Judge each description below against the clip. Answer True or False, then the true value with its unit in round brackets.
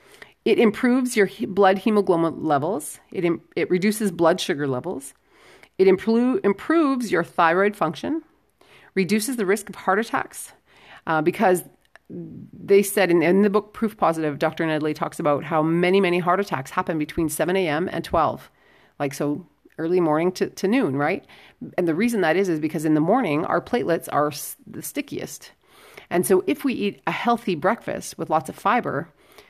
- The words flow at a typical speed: True (170 wpm)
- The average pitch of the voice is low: False (185 Hz)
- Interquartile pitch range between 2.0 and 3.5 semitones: False (4.2 semitones)